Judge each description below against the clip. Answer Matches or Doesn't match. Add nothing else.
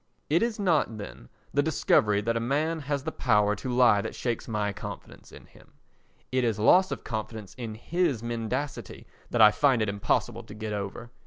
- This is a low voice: Matches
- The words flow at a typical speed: Matches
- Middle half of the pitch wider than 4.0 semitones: Matches